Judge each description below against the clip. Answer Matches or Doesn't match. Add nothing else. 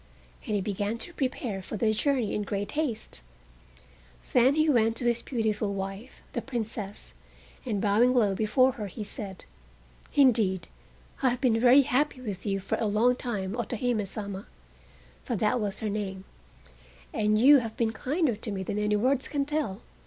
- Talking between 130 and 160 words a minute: Doesn't match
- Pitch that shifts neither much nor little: Matches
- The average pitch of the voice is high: Matches